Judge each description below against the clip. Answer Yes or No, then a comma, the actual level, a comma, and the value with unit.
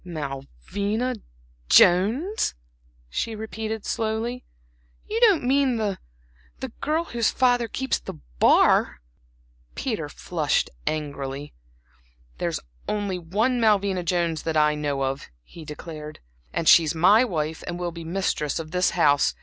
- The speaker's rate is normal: No, slow, 130 wpm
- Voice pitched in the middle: Yes, medium, 180 Hz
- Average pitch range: No, wide, 6.7 semitones